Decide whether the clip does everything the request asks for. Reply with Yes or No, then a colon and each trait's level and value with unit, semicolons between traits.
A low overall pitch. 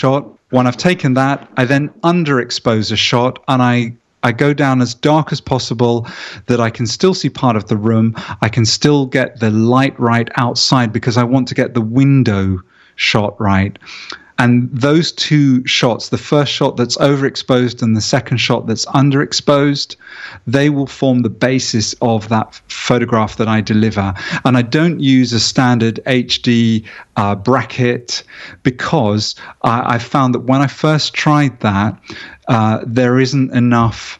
Yes: low, 125 Hz